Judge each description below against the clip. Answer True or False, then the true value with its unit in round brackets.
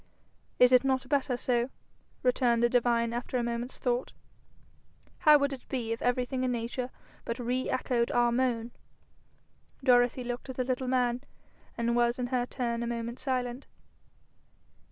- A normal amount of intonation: False (1.3 semitones)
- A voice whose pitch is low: False (245 Hz)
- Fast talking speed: False (155 wpm)